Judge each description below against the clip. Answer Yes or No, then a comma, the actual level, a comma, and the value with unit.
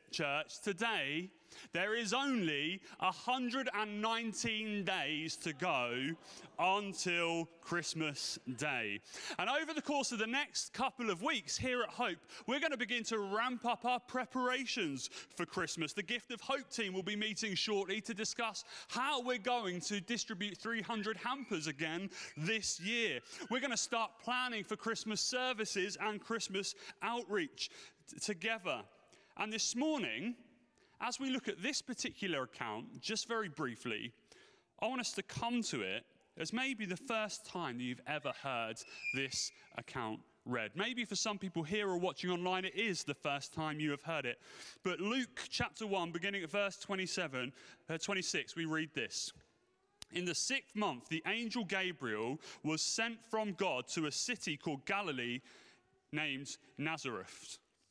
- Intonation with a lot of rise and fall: Yes, wide, 5.9 semitones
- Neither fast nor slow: Yes, average, 155 wpm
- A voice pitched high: Yes, high, 205 Hz